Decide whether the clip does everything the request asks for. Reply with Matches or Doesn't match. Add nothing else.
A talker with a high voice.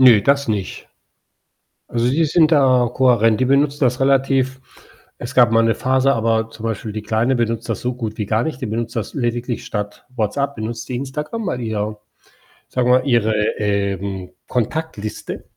Doesn't match